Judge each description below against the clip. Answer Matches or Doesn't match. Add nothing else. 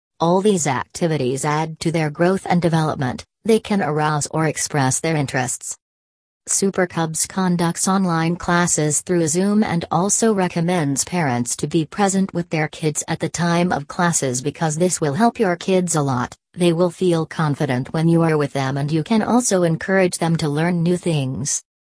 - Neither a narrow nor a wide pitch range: Matches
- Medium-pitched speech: Matches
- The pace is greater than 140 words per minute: Matches